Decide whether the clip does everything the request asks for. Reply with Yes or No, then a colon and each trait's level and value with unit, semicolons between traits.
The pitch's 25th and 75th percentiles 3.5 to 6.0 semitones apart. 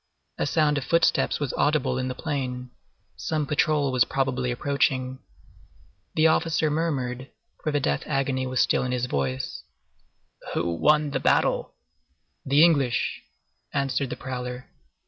No: average, 2.9 semitones